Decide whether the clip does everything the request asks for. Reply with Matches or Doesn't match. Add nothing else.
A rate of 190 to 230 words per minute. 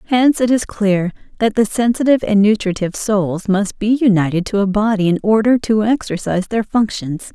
Doesn't match